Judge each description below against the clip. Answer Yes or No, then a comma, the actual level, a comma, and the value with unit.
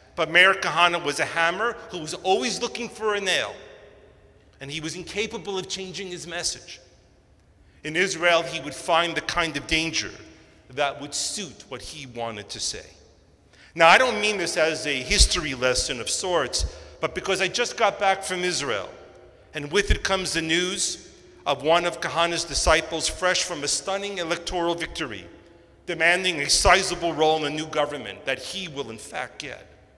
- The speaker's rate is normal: Yes, average, 175 wpm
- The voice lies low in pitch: No, medium, 170 Hz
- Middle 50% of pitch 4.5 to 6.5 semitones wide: No, average, 3.4 semitones